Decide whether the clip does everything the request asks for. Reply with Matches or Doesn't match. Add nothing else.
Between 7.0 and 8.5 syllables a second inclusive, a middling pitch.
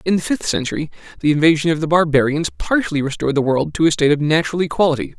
Matches